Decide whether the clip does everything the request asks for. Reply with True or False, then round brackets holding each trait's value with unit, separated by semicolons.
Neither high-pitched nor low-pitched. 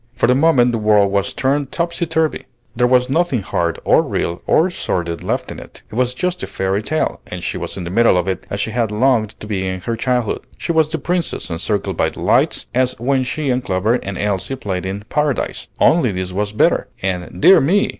False (115 Hz)